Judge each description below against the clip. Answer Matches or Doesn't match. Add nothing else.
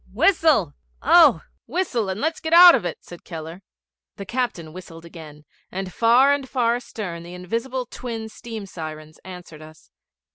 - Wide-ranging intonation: Matches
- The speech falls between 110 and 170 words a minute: Matches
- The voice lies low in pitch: Doesn't match